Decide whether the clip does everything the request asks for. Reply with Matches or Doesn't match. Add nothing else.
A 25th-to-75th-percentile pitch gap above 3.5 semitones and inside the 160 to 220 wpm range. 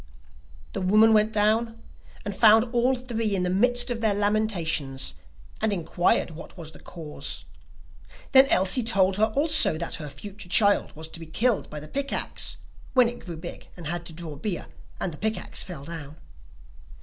Matches